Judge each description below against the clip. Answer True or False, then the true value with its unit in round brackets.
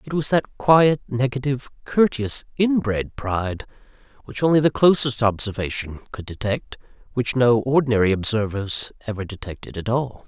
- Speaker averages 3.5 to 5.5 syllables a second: True (5.0 syllables/s)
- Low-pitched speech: True (120 Hz)